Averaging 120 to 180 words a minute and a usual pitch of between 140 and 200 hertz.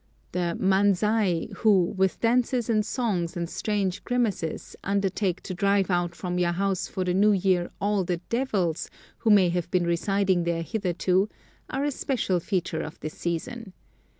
Yes: average, 160 wpm; high, 190 Hz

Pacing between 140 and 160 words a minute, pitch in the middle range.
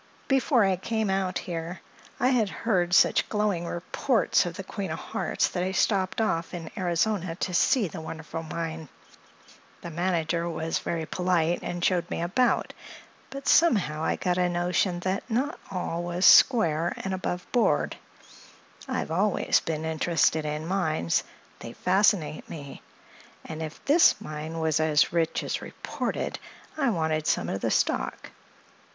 Yes: average, 150 wpm; medium, 175 Hz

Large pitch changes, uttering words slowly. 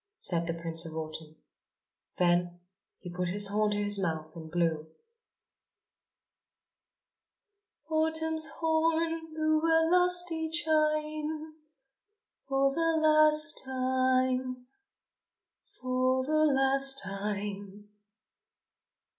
Yes: wide, 8.1 semitones; slow, 90 wpm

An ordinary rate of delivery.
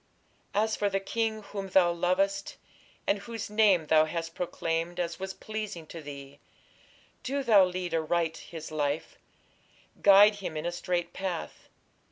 Yes: average, 150 wpm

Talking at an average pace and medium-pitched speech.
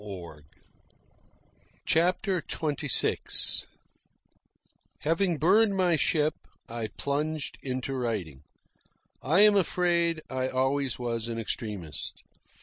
No: slow, 85 wpm; medium, 145 Hz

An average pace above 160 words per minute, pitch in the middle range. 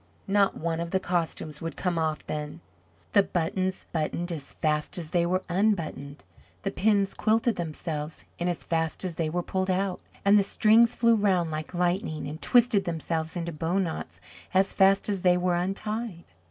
Yes: average, 180 wpm; medium, 175 Hz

